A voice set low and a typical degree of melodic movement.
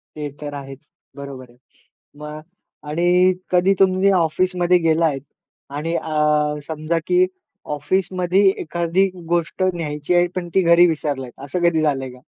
No: medium, 160 Hz; average, 3.1 semitones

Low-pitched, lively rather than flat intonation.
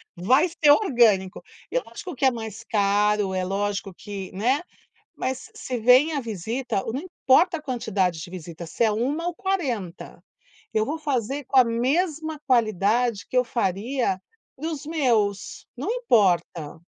No: high, 235 Hz; wide, 6.0 semitones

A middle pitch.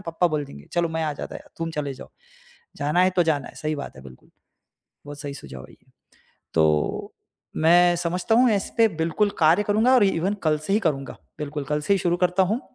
Yes: medium, 165 Hz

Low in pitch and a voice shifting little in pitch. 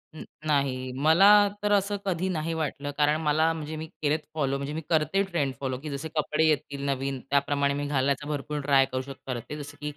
No: medium, 145 Hz; narrow, 2.2 semitones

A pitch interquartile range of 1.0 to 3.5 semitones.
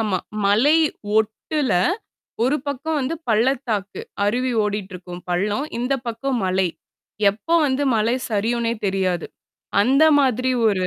No: average, 4.6 semitones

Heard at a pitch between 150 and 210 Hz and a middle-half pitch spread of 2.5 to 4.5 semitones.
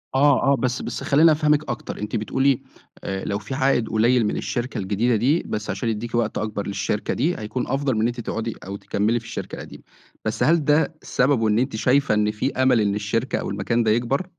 No: low, 120 Hz; average, 4.0 semitones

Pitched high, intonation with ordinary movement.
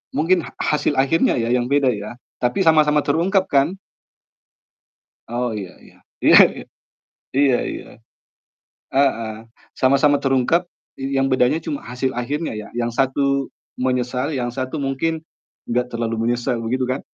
No: low, 130 Hz; average, 3.3 semitones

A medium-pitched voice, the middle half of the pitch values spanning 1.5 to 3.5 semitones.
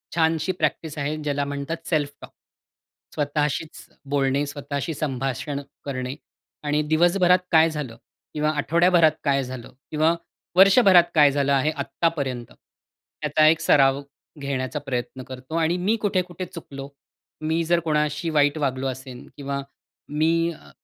Yes: medium, 150 Hz; average, 2.9 semitones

